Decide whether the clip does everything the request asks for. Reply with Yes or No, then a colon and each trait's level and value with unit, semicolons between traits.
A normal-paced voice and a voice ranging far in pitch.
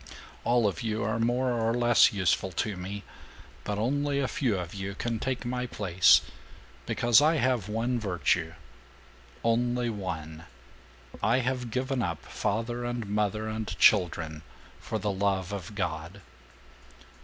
No: average, 145 wpm; average, 4.0 semitones